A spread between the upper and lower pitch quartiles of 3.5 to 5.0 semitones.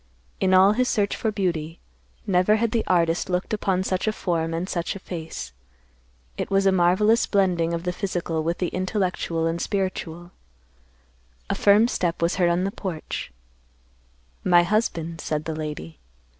No: average, 2.8 semitones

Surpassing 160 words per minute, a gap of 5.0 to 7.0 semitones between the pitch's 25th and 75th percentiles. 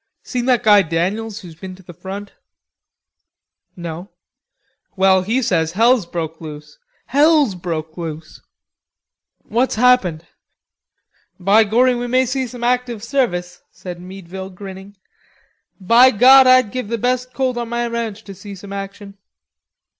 No: average, 140 wpm; average, 5.3 semitones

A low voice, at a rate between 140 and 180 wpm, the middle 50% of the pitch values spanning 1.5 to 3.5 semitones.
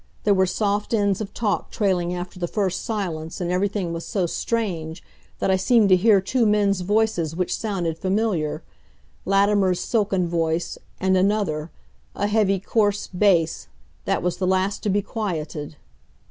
No: high, 190 Hz; average, 160 wpm; average, 2.9 semitones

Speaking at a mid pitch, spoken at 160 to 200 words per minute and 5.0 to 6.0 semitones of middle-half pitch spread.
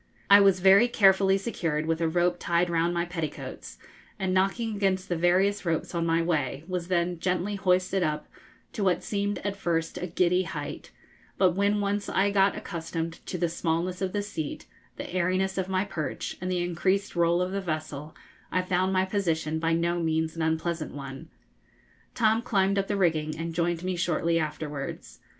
No: medium, 175 Hz; average, 185 wpm; average, 2.7 semitones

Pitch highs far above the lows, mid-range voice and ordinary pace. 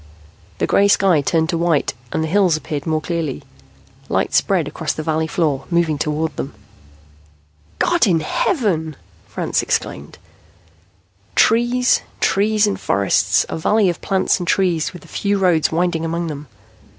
No: average, 3.8 semitones; medium, 165 Hz; average, 150 wpm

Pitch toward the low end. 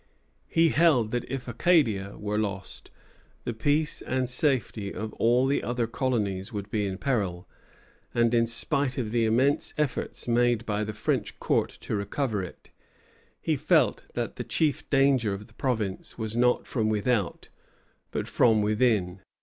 Yes: low, 115 Hz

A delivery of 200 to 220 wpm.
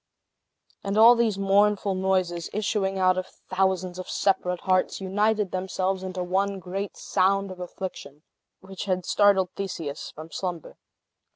No: slow, 135 wpm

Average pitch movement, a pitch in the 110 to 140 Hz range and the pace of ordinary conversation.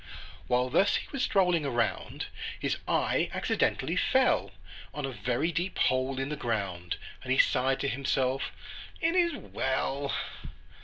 Yes: average, 4.6 semitones; low, 135 Hz; average, 145 wpm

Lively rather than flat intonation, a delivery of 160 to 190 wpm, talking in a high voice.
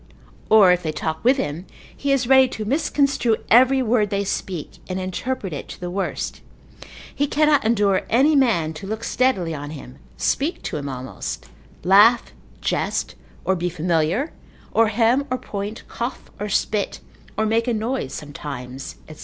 Yes: wide, 6.8 semitones; average, 165 wpm; high, 210 Hz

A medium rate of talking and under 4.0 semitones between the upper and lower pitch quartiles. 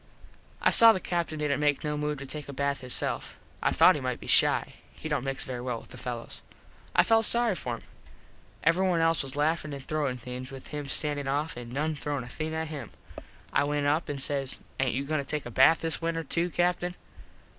No: fast, 225 wpm; average, 3.1 semitones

